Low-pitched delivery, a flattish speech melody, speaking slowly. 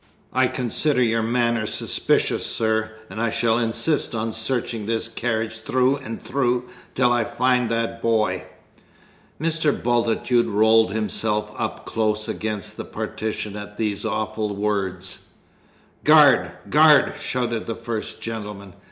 Yes: low, 115 Hz; narrow, 2.0 semitones; slow, 130 wpm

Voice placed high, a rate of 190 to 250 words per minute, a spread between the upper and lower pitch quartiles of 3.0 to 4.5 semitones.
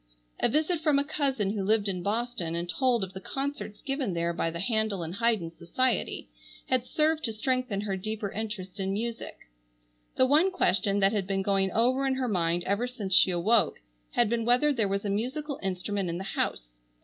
No: high, 215 Hz; average, 200 wpm; average, 4.9 semitones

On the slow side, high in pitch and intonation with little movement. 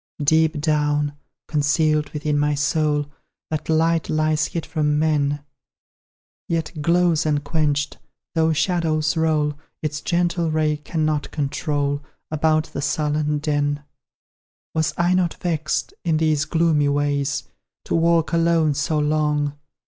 No: slow, 120 wpm; medium, 155 Hz; narrow, 1.6 semitones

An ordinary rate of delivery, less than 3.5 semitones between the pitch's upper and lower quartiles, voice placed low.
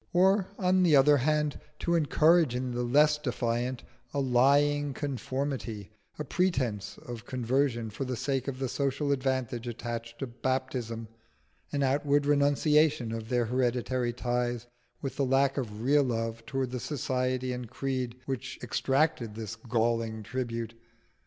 Yes: average, 145 wpm; average, 3.1 semitones; low, 130 Hz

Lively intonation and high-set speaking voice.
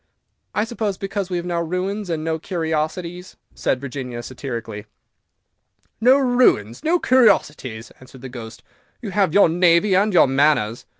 No: wide, 7.3 semitones; medium, 170 Hz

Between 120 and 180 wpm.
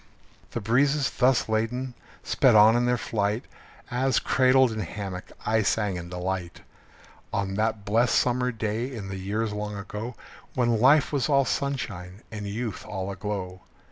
Yes: average, 155 wpm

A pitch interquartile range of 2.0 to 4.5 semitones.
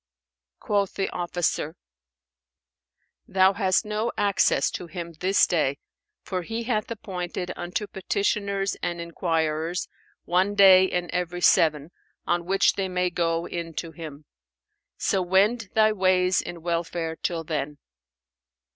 Yes: narrow, 2.5 semitones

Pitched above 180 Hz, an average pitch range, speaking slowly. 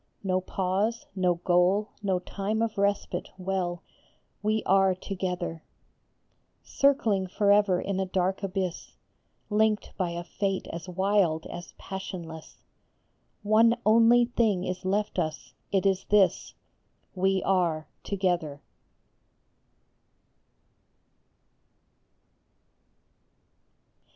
No: high, 190 Hz; narrow, 2.3 semitones; slow, 95 wpm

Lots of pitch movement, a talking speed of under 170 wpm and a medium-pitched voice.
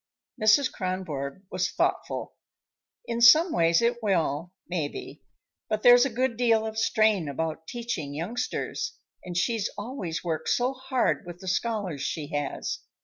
No: wide, 6.2 semitones; average, 145 wpm; high, 205 Hz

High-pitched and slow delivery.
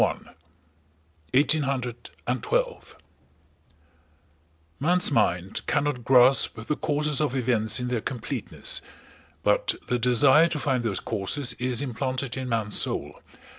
No: low, 125 Hz; slow, 125 wpm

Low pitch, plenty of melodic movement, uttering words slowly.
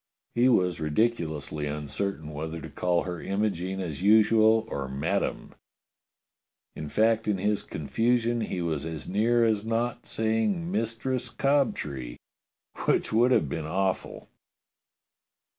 Yes: low, 100 Hz; wide, 6.4 semitones; slow, 125 wpm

